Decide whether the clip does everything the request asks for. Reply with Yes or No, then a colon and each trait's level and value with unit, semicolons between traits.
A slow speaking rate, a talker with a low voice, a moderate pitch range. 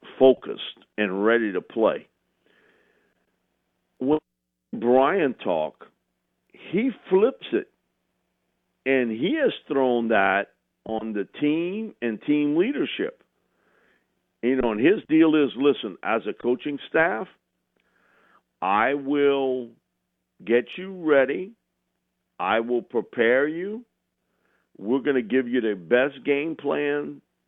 Yes: slow, 110 wpm; low, 130 Hz; average, 4.9 semitones